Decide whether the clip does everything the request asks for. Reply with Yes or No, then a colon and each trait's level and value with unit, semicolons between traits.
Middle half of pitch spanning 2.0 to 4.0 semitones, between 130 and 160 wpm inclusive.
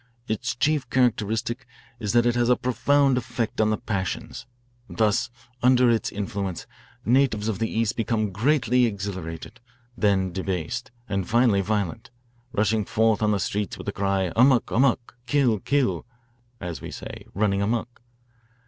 Yes: average, 3.3 semitones; average, 155 wpm